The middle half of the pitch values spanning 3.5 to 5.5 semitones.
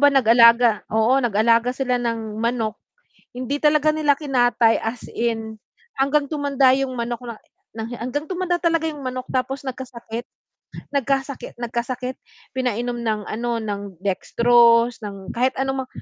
No: average, 2.7 semitones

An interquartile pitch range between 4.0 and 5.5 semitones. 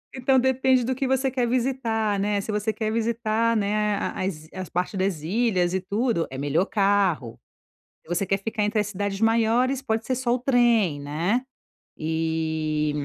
Yes: average, 4.8 semitones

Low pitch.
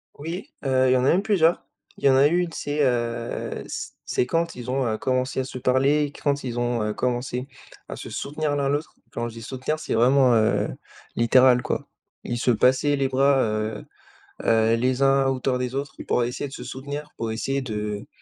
Yes: low, 130 Hz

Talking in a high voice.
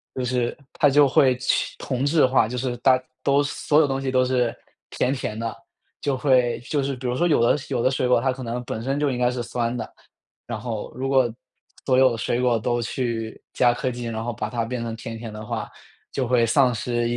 No: low, 125 Hz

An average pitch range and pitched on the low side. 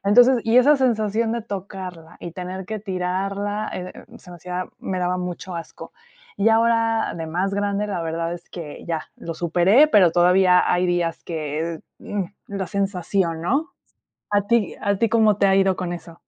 No: average, 3.1 semitones; high, 190 Hz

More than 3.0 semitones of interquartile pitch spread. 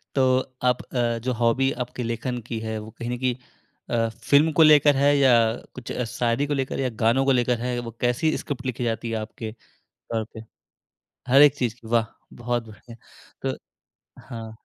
No: narrow, 2.4 semitones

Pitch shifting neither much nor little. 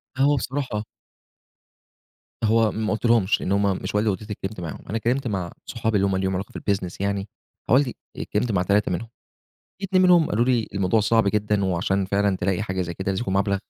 Yes: average, 3.0 semitones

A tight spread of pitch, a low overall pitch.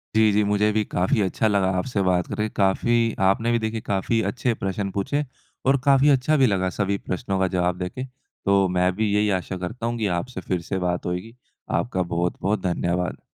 No: average, 3.7 semitones; low, 100 Hz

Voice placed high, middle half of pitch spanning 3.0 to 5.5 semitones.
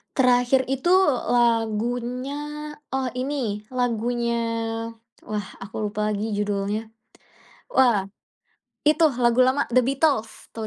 Yes: high, 240 Hz; average, 3.4 semitones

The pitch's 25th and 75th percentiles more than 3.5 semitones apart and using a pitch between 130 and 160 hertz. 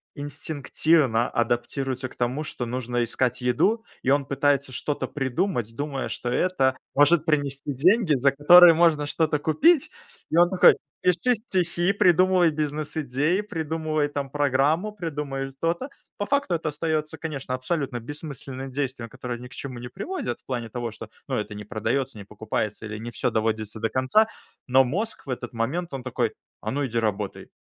Yes: average, 4.8 semitones; medium, 140 Hz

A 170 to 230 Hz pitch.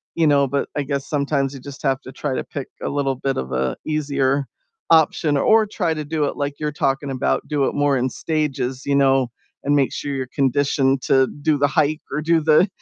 No: medium, 140 Hz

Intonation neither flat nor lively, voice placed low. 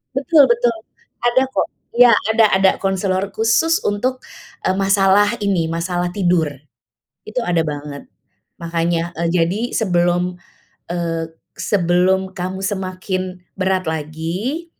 No: average, 3.1 semitones; medium, 185 Hz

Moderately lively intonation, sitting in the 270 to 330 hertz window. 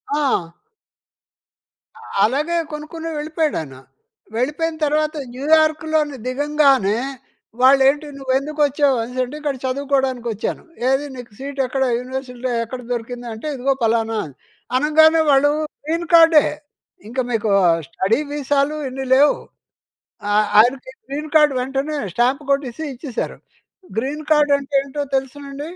Yes: average, 3.2 semitones; very high, 275 Hz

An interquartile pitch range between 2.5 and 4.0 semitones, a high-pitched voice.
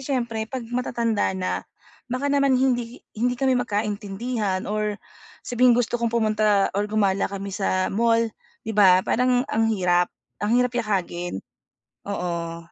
Yes: average, 3.7 semitones; high, 220 Hz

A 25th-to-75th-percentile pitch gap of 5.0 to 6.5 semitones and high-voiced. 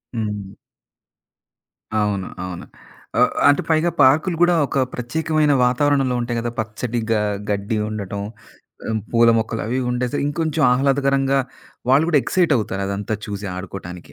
No: wide, 5.6 semitones; low, 120 Hz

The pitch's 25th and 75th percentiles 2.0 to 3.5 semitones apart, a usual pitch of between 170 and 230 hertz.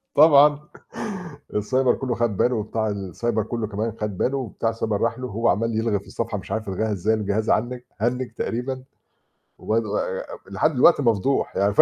No: average, 3.1 semitones; low, 115 Hz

